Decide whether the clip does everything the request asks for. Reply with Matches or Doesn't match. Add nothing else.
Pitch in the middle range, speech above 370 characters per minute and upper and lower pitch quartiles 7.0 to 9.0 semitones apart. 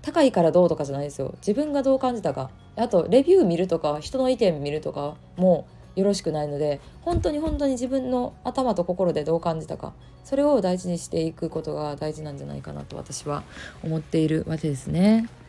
Matches